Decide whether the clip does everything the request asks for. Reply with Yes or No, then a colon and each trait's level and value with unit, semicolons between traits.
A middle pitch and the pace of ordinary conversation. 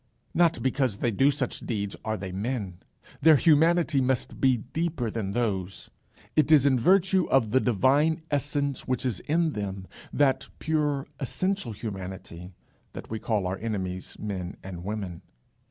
No: low, 125 Hz; average, 155 wpm